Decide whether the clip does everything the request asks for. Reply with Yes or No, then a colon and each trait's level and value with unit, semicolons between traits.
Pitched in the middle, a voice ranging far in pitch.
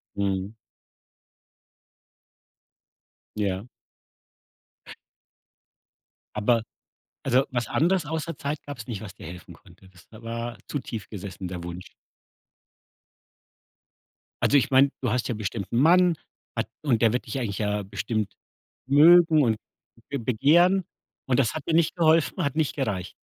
No: low, 120 Hz; wide, 6.1 semitones